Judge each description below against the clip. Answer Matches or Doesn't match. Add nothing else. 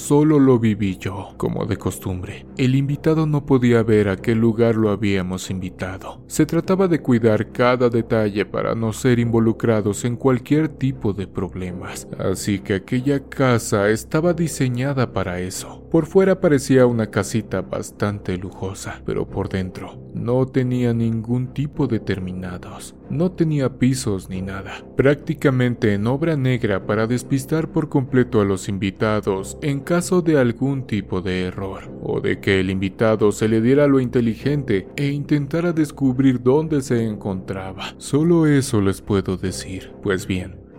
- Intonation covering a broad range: Matches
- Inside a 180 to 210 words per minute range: Doesn't match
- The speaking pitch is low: Matches